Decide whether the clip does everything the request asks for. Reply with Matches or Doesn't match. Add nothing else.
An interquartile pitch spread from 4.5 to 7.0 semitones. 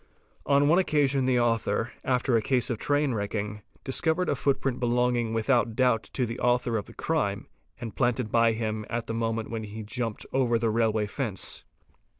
Doesn't match